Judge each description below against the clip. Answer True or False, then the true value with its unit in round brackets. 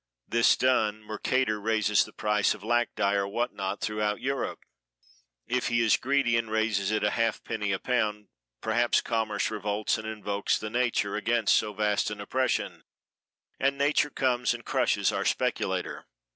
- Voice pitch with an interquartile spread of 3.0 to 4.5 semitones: False (2.4 semitones)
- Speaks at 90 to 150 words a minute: False (160 wpm)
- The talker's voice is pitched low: True (110 Hz)